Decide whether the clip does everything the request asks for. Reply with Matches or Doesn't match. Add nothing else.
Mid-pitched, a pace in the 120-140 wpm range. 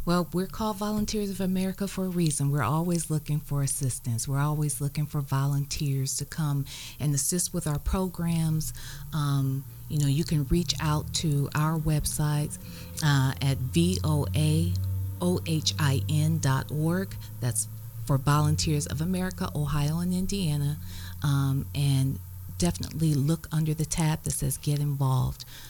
Matches